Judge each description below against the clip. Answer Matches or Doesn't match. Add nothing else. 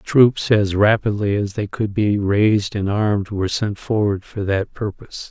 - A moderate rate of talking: Matches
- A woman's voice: Doesn't match